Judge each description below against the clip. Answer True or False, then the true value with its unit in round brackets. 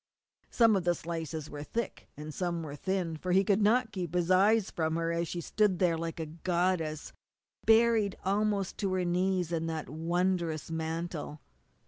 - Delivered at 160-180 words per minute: True (175 wpm)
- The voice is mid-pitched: True (175 Hz)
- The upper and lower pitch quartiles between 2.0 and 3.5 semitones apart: True (2.9 semitones)